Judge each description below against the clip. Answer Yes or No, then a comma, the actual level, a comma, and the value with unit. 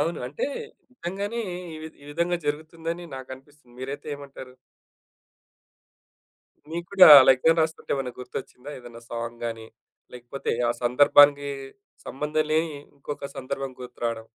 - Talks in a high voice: No, medium, 140 Hz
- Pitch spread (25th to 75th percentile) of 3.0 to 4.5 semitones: Yes, average, 3.9 semitones